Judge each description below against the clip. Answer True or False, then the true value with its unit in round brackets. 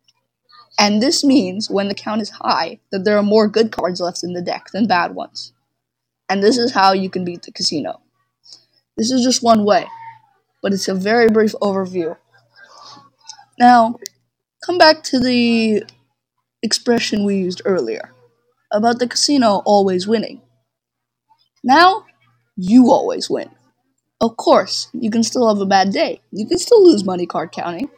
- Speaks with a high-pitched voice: True (225 Hz)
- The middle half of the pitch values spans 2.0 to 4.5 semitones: False (5.1 semitones)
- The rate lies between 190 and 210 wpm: False (160 wpm)